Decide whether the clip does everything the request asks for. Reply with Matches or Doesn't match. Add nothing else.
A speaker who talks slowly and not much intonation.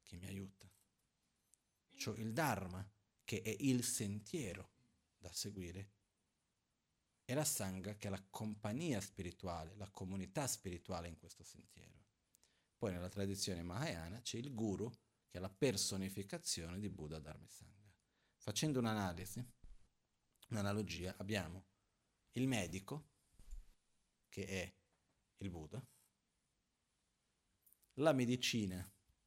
Doesn't match